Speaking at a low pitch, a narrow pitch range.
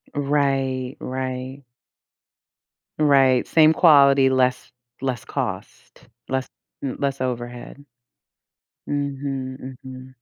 Yes: low, 130 Hz; narrow, 1.5 semitones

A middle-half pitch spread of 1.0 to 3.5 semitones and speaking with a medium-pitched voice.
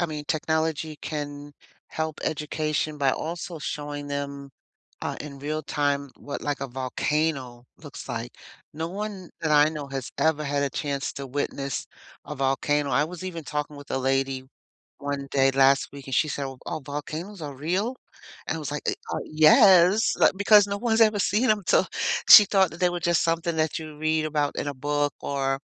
Yes: average, 2.7 semitones; medium, 150 Hz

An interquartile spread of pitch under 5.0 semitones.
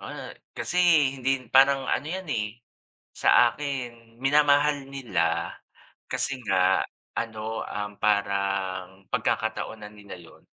No: wide, 5.4 semitones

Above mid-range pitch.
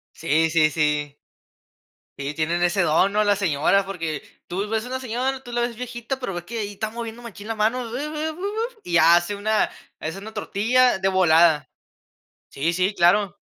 Yes: high, 200 Hz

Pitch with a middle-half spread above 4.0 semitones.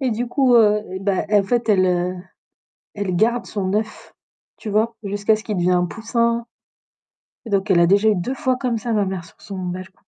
No: average, 3.7 semitones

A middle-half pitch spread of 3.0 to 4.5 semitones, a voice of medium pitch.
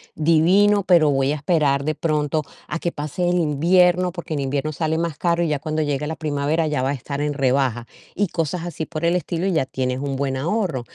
Yes: average, 3.3 semitones; medium, 155 Hz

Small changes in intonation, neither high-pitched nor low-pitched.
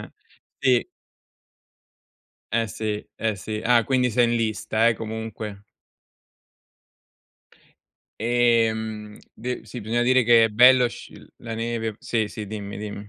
No: narrow, 1.8 semitones; low, 115 Hz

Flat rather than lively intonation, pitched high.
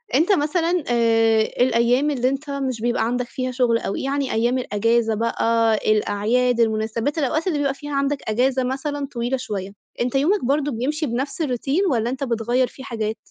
No: average, 3.4 semitones; very high, 250 Hz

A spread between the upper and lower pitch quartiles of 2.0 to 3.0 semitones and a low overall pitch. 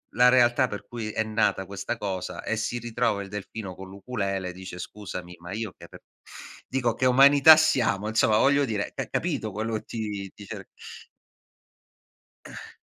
No: average, 3.6 semitones; low, 110 Hz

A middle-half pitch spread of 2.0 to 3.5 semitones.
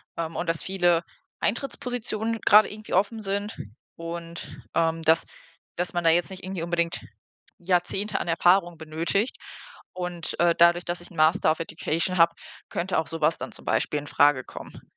Yes: narrow, 2.6 semitones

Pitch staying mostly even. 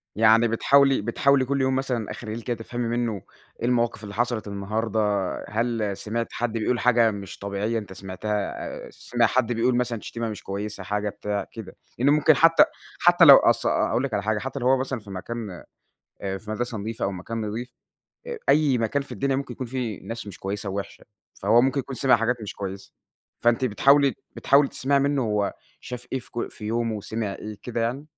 No: average, 3.5 semitones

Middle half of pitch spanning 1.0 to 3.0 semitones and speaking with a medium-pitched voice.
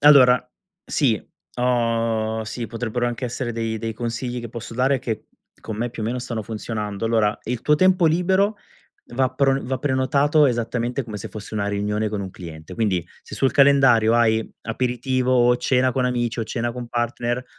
No: narrow, 2.5 semitones; low, 120 Hz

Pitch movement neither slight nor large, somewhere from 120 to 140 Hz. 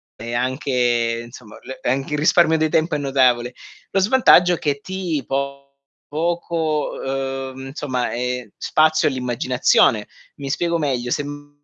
Yes: average, 3.8 semitones; low, 135 Hz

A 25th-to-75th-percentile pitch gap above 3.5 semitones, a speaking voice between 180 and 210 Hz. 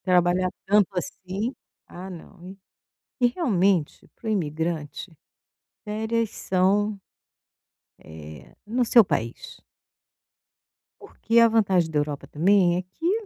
Yes: average, 4.1 semitones; high, 190 Hz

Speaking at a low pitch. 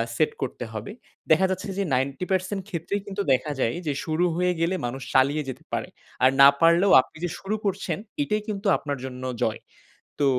No: medium, 165 Hz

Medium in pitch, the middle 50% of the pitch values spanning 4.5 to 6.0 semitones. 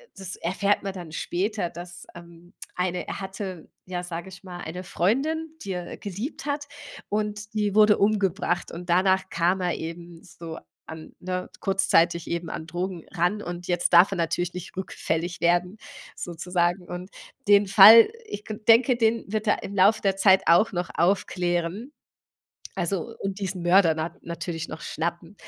No: medium, 180 Hz; narrow, 2.6 semitones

